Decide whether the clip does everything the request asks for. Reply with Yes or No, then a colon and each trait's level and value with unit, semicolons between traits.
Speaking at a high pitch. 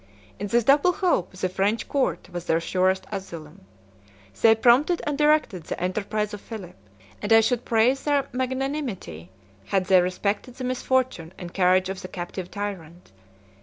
Yes: high, 205 Hz